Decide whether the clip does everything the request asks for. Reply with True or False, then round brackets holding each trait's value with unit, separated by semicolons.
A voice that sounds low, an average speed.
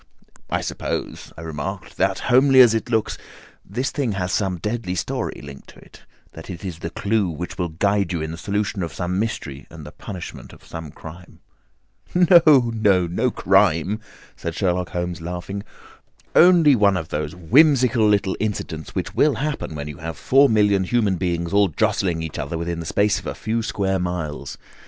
True (95 Hz; 185 wpm)